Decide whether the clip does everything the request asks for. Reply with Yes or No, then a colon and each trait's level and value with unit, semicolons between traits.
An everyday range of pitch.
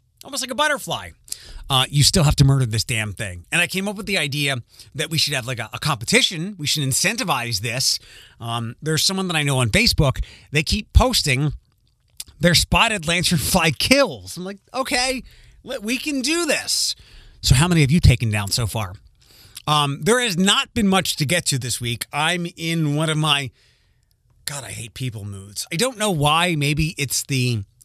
No: wide, 6.9 semitones